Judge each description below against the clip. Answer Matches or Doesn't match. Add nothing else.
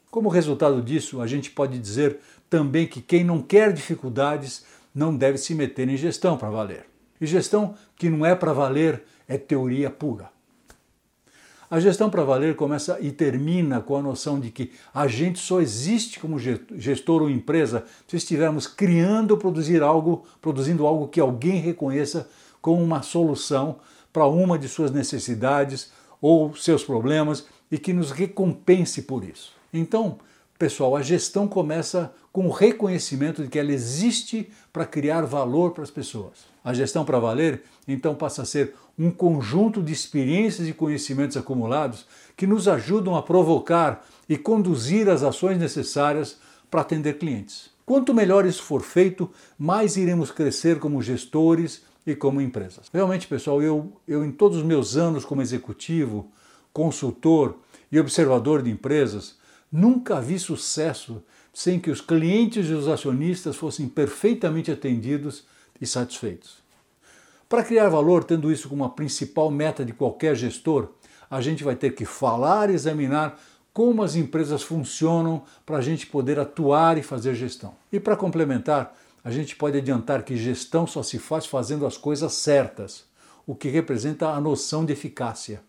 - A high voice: Doesn't match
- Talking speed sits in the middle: Matches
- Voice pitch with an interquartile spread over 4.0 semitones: Doesn't match